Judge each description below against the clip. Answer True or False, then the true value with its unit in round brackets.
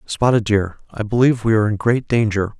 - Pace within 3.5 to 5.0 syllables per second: False (6.1 syllables/s)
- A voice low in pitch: True (110 Hz)